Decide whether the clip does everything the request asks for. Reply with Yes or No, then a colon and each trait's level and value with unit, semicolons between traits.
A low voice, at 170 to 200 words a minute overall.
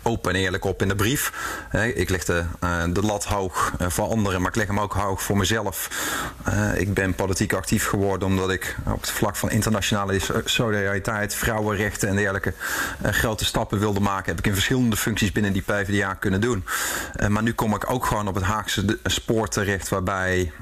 Yes: low, 100 Hz; average, 190 wpm